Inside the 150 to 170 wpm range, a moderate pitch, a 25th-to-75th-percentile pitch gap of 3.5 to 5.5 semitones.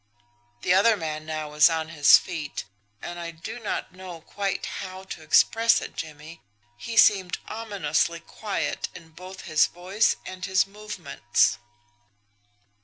No: average, 140 wpm; medium, 180 Hz; average, 3.8 semitones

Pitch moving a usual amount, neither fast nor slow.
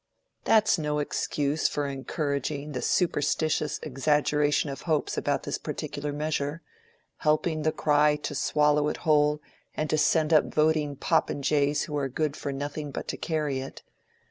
No: narrow, 1.2 semitones; average, 155 wpm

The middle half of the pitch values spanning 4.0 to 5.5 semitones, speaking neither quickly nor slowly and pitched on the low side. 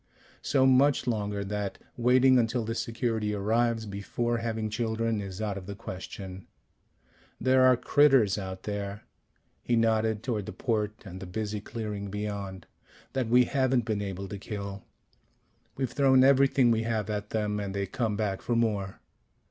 No: average, 2.8 semitones; average, 165 wpm; low, 110 Hz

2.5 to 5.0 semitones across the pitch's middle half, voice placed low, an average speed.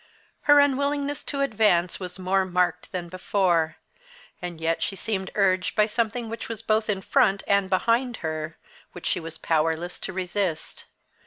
No: average, 4.3 semitones; high, 190 Hz; average, 160 wpm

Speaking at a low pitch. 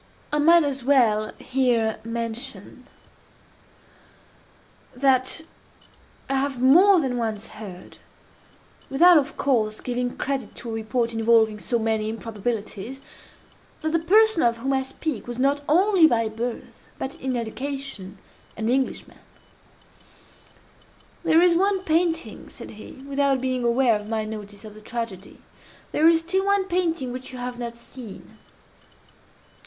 No: very high, 250 Hz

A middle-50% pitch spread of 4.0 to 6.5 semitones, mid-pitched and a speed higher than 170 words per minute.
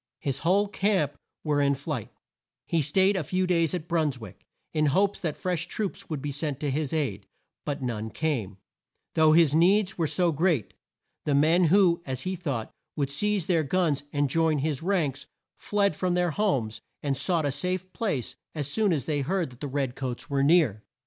Yes: average, 4.5 semitones; medium, 155 Hz; average, 195 wpm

